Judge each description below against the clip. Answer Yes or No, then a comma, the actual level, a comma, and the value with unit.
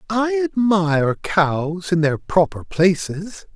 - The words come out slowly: Yes, slow, 120 wpm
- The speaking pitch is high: No, medium, 180 Hz